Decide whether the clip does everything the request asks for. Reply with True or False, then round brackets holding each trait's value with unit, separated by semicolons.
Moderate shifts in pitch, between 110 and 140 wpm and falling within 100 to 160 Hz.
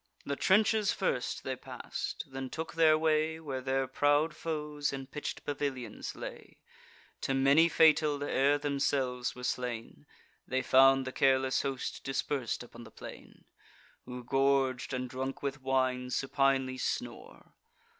False (2.1 semitones; 135 wpm; 135 Hz)